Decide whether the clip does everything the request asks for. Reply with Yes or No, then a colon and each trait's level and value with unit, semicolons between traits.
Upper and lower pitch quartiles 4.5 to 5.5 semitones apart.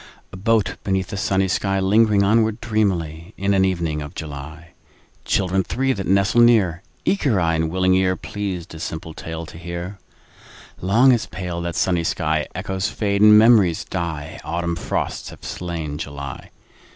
No: average, 3.5 semitones